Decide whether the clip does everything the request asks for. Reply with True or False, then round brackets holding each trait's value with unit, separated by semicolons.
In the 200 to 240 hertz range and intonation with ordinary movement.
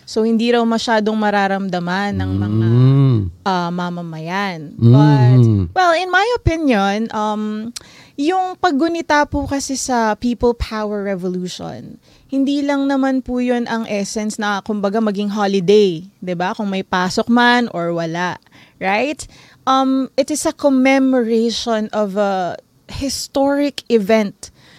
False (215 Hz; 6.1 semitones)